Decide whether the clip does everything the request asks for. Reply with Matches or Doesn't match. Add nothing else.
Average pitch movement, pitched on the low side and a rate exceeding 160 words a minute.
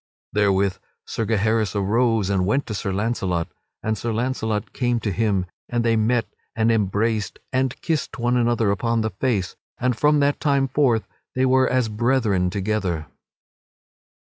Doesn't match